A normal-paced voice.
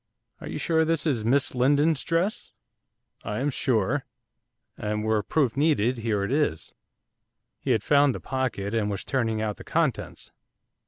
Yes: average, 160 wpm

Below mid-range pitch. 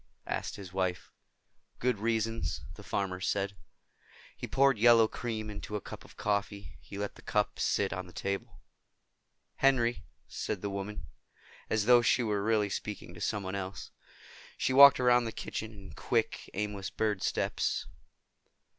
Yes: low, 105 Hz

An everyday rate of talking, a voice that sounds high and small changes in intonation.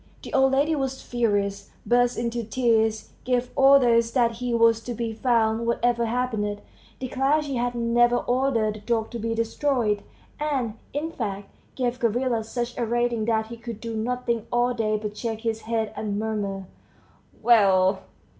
Yes: average, 165 wpm; high, 235 Hz; narrow, 2.0 semitones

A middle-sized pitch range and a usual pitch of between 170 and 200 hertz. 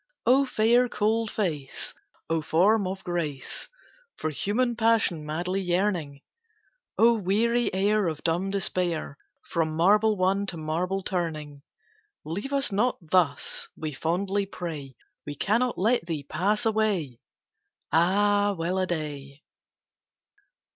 Yes: average, 4.8 semitones; medium, 185 Hz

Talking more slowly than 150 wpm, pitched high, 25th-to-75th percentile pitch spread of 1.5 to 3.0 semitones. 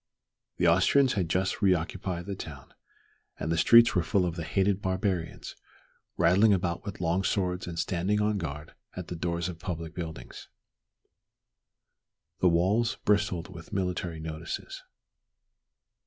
No: average, 140 wpm; very low, 90 Hz; average, 2.7 semitones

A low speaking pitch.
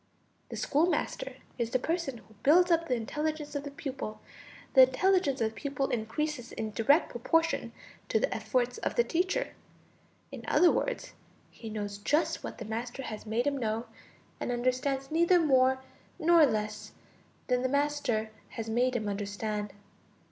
No: very high, 260 Hz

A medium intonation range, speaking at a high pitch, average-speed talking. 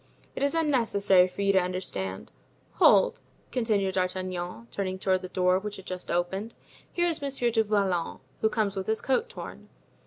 Yes: average, 3.7 semitones; high, 195 Hz; average, 175 wpm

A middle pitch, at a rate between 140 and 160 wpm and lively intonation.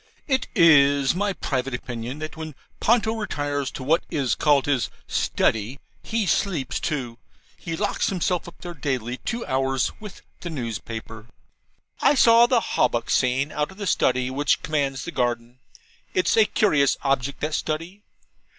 Yes: medium, 145 Hz; average, 155 wpm; wide, 5.8 semitones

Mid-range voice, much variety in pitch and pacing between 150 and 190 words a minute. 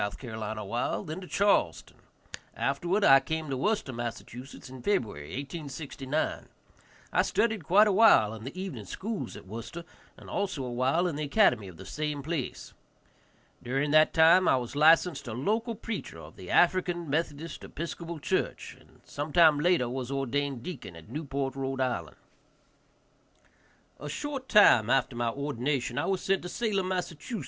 Yes: medium, 145 Hz; wide, 5.9 semitones; average, 155 wpm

